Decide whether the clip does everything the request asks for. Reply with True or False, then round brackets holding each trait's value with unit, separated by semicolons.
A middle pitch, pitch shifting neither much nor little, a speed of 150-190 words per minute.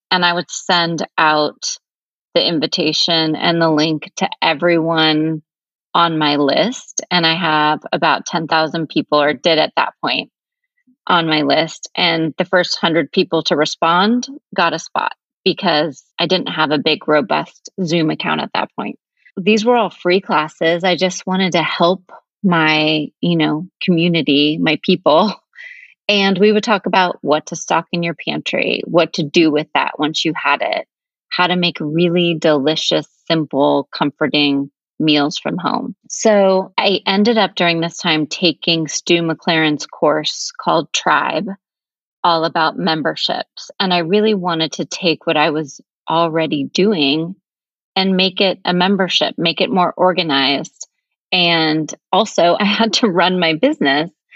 True (170 Hz; 3.2 semitones; 155 wpm)